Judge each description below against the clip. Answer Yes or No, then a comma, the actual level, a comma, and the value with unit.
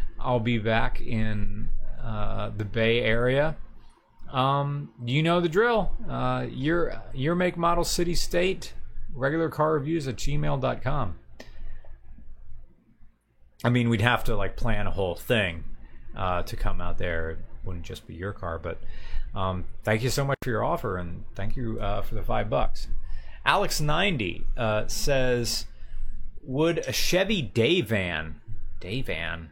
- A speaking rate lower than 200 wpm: Yes, average, 140 wpm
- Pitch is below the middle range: Yes, low, 115 Hz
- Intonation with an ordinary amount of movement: No, wide, 5.7 semitones